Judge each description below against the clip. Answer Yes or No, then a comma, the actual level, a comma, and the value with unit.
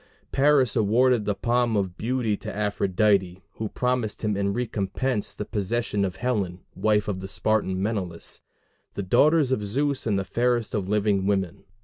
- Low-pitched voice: Yes, low, 105 Hz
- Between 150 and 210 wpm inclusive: Yes, average, 160 wpm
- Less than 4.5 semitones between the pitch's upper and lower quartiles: Yes, average, 3.6 semitones